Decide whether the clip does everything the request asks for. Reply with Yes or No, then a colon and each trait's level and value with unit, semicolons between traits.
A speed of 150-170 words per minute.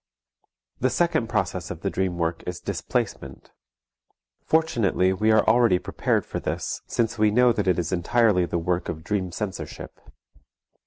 Yes: average, 155 wpm